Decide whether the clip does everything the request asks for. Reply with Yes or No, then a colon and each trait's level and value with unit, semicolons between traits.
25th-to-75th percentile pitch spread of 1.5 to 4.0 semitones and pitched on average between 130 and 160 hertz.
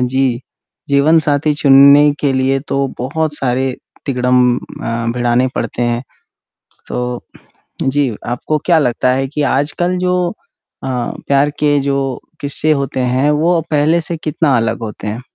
Yes: average, 3.0 semitones; low, 135 Hz